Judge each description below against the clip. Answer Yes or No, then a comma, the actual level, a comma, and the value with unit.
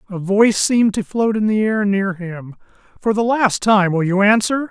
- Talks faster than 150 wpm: Yes, fast, 205 wpm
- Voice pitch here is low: No, high, 205 Hz